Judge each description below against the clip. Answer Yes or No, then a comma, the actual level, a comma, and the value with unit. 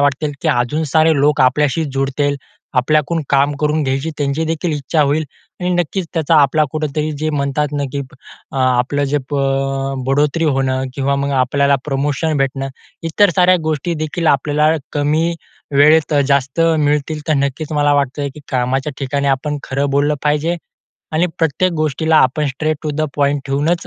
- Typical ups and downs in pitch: No, narrow, 2.2 semitones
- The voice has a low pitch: No, medium, 145 Hz